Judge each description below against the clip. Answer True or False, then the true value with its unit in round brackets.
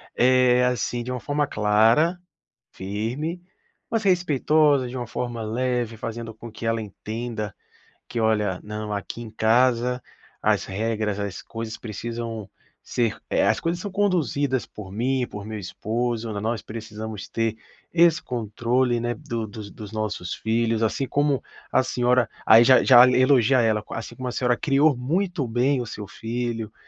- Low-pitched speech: True (120 Hz)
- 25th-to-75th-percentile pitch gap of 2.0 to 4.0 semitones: True (2.8 semitones)